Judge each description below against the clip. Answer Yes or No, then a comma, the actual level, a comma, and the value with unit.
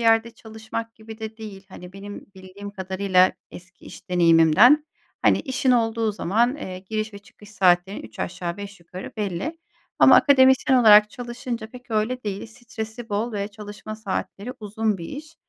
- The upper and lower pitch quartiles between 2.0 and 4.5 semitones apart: Yes, average, 3.2 semitones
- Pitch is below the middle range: No, high, 215 Hz